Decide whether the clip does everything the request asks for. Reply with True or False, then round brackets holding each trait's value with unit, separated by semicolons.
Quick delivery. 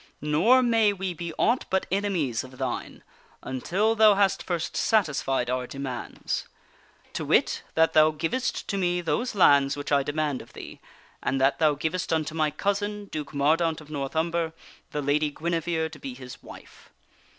False (180 wpm)